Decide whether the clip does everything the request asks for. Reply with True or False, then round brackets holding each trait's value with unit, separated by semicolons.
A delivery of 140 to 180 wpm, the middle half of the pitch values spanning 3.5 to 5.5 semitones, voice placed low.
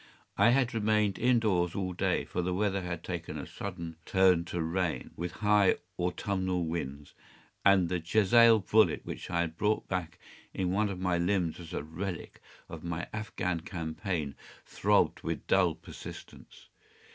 False (160 wpm; 2.9 semitones; 90 Hz)